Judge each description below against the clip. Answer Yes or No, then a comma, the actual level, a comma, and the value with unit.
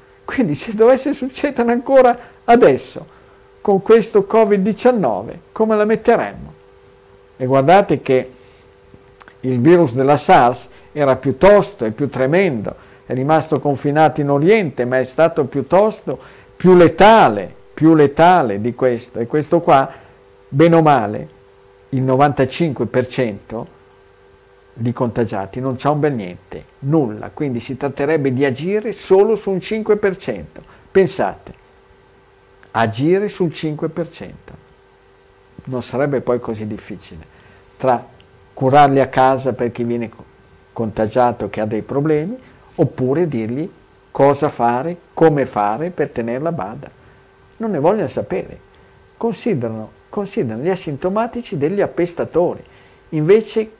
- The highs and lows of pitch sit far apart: Yes, wide, 8.1 semitones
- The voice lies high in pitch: No, low, 135 Hz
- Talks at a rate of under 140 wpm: Yes, slow, 115 wpm